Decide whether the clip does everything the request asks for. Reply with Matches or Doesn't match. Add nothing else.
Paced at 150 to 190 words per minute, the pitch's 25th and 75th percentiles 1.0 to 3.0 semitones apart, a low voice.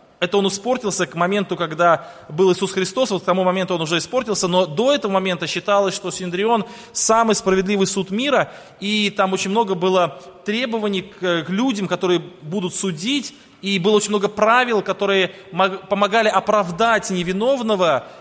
Doesn't match